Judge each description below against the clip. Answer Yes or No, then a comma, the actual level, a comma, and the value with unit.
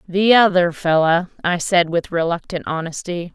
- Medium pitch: Yes, medium, 175 Hz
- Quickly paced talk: No, average, 145 wpm